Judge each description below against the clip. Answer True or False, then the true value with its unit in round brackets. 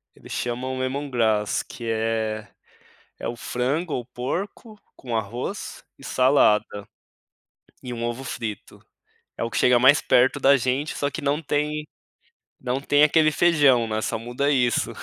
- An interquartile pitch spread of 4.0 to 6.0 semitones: False (3.6 semitones)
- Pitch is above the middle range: False (125 Hz)